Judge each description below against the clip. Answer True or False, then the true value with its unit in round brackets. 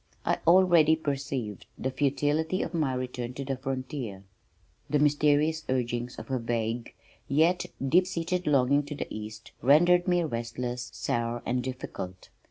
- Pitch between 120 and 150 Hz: True (135 Hz)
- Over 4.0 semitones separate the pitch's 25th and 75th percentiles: True (4.5 semitones)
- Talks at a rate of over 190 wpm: False (145 wpm)